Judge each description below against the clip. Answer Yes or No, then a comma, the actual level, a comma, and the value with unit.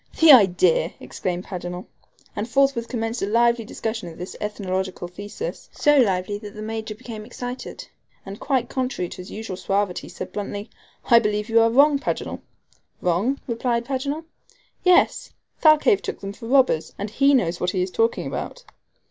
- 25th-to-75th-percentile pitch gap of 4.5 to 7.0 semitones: Yes, average, 4.8 semitones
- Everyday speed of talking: Yes, average, 165 wpm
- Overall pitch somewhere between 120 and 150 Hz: No, high, 220 Hz